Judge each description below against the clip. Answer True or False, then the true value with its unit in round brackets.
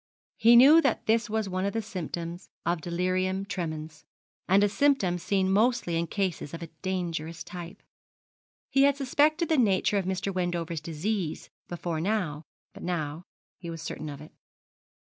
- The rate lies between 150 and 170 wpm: True (165 wpm)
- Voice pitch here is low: False (185 Hz)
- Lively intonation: False (4.1 semitones)